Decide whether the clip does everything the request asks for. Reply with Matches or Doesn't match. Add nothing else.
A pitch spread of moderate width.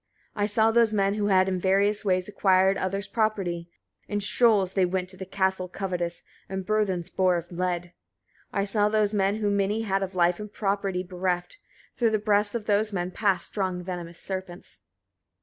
Doesn't match